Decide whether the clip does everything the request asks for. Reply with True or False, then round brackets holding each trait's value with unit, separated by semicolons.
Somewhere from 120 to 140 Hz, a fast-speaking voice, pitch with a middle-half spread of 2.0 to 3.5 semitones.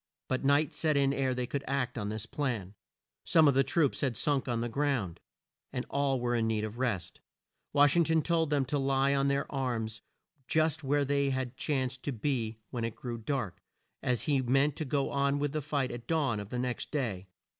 True (135 Hz; 210 wpm; 3.0 semitones)